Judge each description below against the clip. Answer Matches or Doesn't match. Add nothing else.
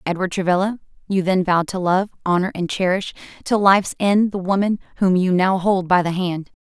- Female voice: Matches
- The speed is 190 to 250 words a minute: Matches